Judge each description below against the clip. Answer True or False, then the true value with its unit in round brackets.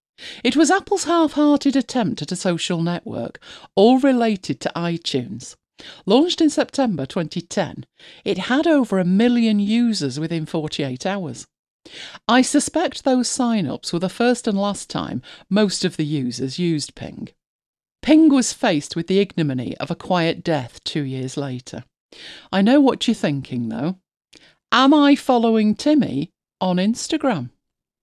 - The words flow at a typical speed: True (145 wpm)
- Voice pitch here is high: True (205 Hz)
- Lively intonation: True (7.7 semitones)